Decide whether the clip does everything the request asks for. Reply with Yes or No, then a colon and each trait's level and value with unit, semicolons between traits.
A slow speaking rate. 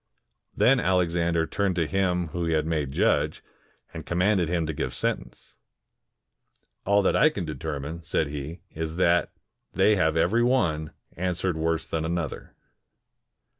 No: average, 150 wpm